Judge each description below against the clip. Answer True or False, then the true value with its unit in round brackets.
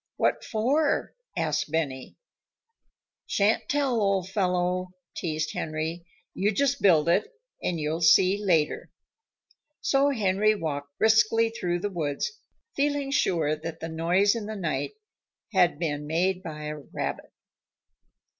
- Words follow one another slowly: True (125 wpm)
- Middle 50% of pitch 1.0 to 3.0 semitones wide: False (5.2 semitones)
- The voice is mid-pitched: True (180 Hz)